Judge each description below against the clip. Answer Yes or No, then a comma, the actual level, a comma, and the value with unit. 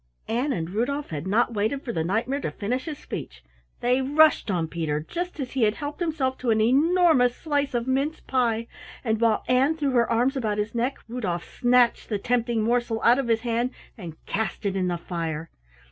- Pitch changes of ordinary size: Yes, average, 4.2 semitones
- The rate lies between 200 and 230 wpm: Yes, fast, 205 wpm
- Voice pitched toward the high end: Yes, high, 240 Hz